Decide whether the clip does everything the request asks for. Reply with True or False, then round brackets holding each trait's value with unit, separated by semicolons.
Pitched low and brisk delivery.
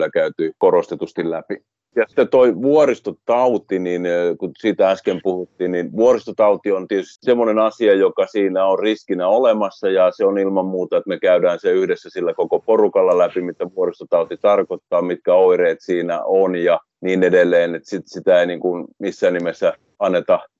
True (110 Hz; 165 wpm)